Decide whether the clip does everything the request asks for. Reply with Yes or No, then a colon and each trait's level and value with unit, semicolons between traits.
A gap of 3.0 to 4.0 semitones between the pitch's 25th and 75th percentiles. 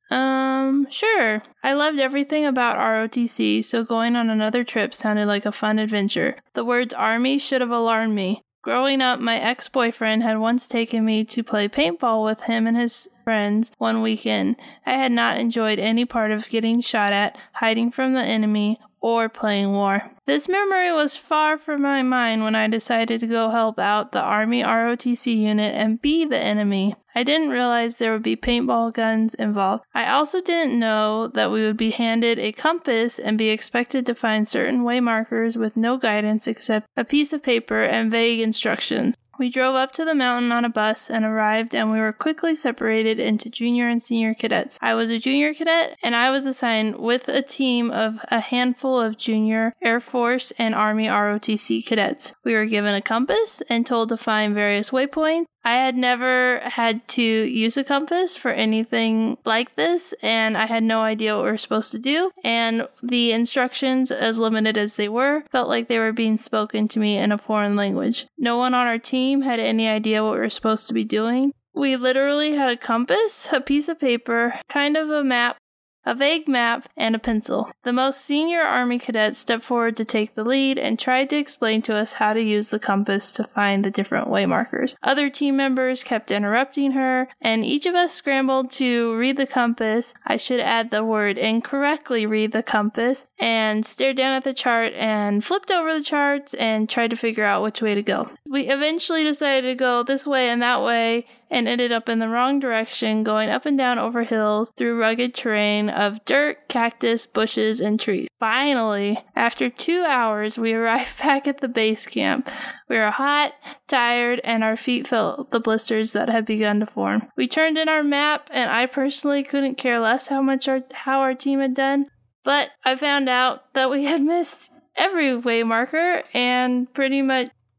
Yes: average, 3.3 semitones